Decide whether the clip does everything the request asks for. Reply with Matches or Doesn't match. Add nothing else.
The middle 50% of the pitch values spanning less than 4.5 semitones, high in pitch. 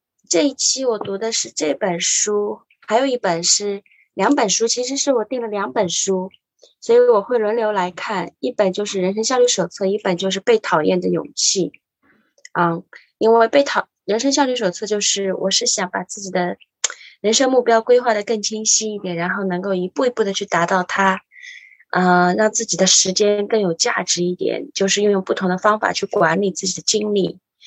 Matches